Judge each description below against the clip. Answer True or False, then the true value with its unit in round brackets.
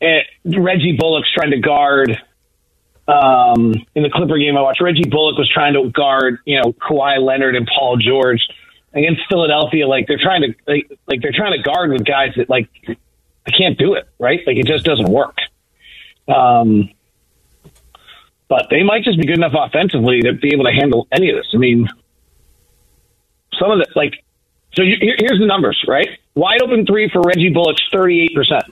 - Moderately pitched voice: True (145 Hz)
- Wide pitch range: True (5.8 semitones)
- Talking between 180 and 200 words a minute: True (190 wpm)